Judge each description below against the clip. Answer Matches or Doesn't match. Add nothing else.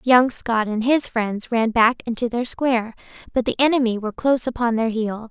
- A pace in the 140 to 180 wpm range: Doesn't match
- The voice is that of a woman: Matches